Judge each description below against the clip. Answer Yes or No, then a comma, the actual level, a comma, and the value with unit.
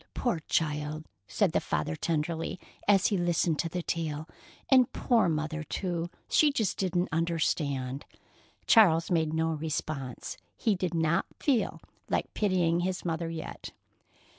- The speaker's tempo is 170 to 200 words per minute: No, average, 140 wpm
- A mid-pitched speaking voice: Yes, medium, 165 Hz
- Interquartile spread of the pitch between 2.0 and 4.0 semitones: Yes, average, 2.7 semitones